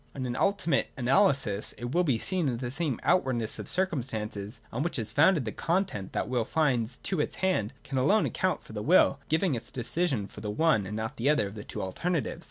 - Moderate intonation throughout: No, wide, 6.9 semitones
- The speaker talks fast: Yes, fast, 225 wpm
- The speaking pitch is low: Yes, low, 130 Hz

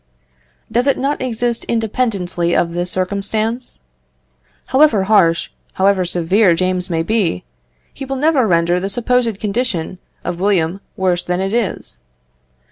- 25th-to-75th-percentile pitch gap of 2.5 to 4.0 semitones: No, average, 4.9 semitones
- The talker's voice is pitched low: No, high, 195 Hz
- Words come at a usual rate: No, slow, 130 wpm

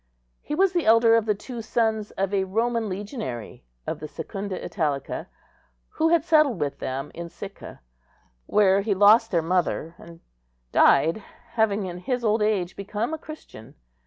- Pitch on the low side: No, high, 205 Hz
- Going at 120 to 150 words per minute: No, average, 160 wpm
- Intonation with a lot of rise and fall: No, average, 4.4 semitones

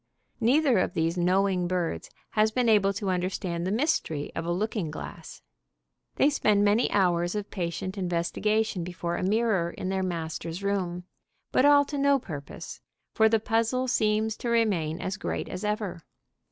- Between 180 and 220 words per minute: No, average, 165 wpm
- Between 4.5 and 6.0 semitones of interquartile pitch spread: No, average, 4.0 semitones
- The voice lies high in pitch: Yes, high, 195 Hz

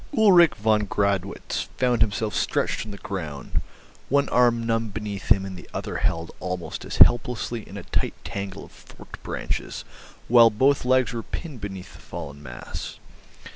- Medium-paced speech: Yes, average, 165 wpm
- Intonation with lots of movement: No, average, 3.8 semitones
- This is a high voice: No, low, 105 Hz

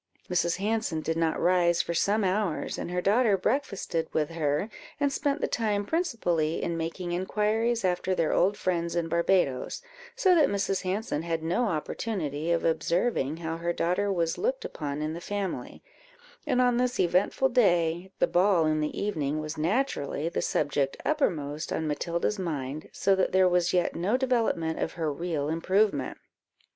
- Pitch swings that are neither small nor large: Yes, average, 4.4 semitones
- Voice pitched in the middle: Yes, medium, 175 Hz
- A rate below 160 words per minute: No, average, 170 wpm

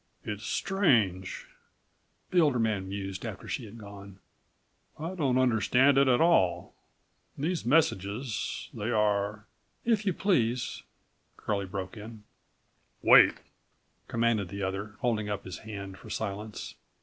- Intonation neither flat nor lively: Yes, average, 4.5 semitones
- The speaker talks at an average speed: No, slow, 125 wpm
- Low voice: Yes, low, 110 Hz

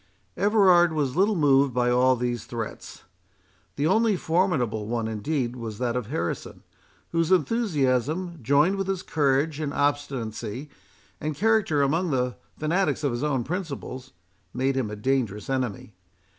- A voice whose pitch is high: No, medium, 140 Hz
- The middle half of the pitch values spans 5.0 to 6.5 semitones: Yes, average, 5.3 semitones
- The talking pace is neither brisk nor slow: Yes, average, 145 wpm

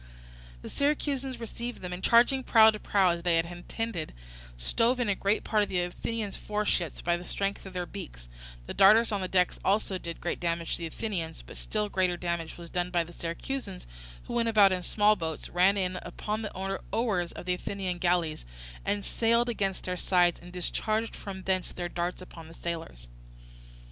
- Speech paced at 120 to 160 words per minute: No, average, 195 wpm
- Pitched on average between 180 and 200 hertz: Yes, medium, 185 Hz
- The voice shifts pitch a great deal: No, average, 3.6 semitones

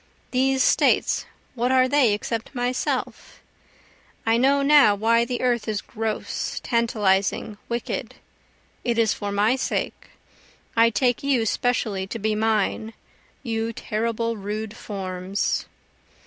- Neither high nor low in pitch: No, high, 230 Hz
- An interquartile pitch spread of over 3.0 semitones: No, narrow, 2.6 semitones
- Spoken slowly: Yes, slow, 120 wpm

